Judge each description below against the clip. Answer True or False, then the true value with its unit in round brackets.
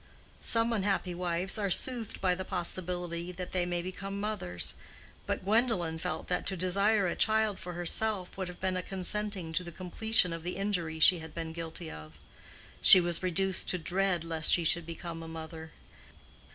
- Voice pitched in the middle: True (180 Hz)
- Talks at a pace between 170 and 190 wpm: True (180 wpm)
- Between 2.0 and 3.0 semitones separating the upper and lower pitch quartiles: True (2.7 semitones)